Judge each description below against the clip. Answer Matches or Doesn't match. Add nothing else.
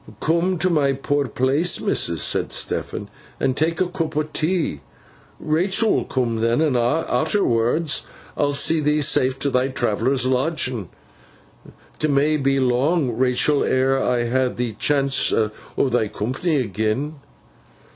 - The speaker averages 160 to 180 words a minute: Doesn't match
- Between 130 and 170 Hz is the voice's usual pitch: Matches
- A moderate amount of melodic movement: Matches